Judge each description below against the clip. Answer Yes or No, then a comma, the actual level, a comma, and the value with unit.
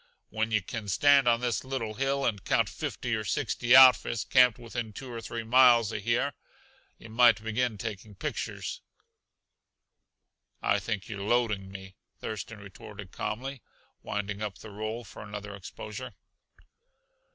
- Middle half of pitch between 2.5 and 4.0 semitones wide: Yes, average, 2.9 semitones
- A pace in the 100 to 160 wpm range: Yes, average, 145 wpm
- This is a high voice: No, low, 110 Hz